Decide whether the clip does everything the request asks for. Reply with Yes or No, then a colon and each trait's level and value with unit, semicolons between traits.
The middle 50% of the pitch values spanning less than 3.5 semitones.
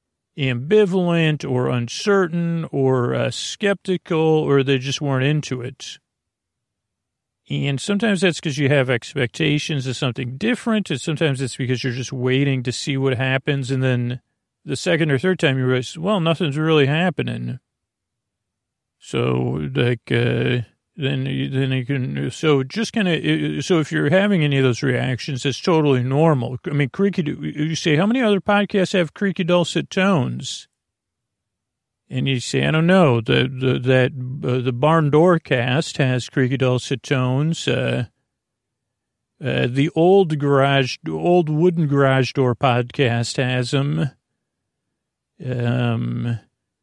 No: average, 4.3 semitones